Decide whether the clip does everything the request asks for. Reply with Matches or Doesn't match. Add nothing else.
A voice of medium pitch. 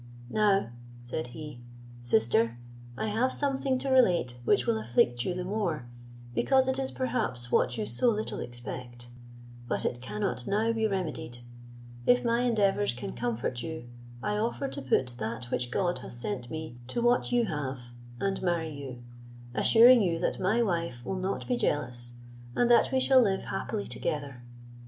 Matches